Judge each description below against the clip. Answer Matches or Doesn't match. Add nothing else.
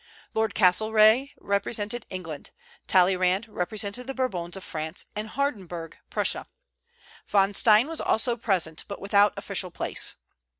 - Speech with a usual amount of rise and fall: Matches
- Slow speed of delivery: Matches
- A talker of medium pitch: Doesn't match